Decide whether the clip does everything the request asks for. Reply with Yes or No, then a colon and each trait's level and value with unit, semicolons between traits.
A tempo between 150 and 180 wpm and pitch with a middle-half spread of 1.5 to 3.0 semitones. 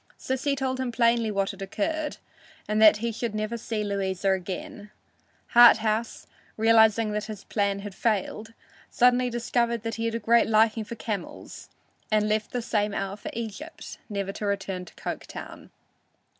Yes: average, 160 wpm; narrow, 2.4 semitones